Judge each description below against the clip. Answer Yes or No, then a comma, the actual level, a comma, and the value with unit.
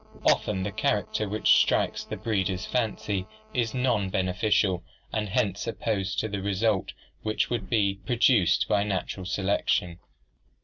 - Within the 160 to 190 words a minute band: No, slow, 135 wpm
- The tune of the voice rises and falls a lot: No, narrow, 2.6 semitones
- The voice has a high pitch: No, low, 100 Hz